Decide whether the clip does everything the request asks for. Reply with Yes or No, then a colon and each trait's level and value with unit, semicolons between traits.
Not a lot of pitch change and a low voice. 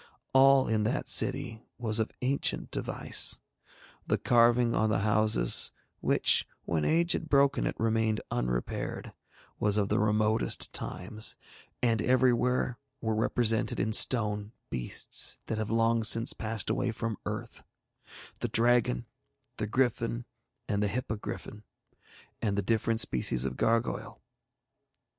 Yes: narrow, 2.1 semitones; low, 110 Hz